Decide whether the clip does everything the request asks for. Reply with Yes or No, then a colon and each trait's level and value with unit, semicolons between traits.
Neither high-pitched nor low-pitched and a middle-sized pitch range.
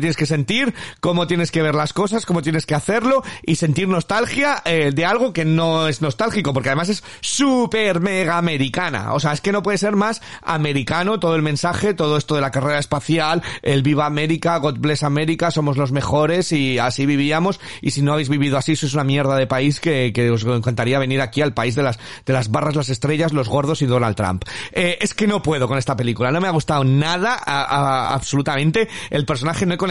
Yes: medium, 150 Hz; average, 4.0 semitones